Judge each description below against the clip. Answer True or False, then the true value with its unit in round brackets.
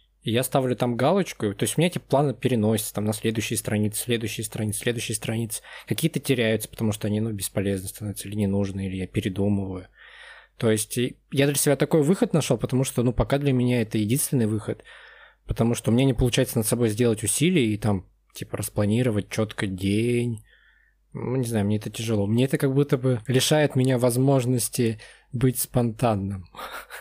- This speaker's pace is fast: True (185 wpm)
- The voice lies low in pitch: True (115 Hz)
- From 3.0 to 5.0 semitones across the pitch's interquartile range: True (3.4 semitones)